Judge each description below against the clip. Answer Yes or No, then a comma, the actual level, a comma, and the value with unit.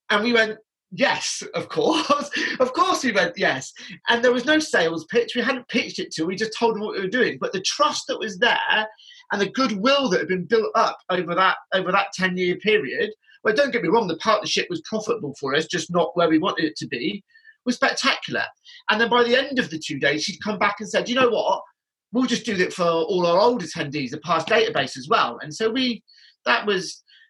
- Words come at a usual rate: No, fast, 235 wpm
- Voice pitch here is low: No, high, 220 Hz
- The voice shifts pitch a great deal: Yes, wide, 6.2 semitones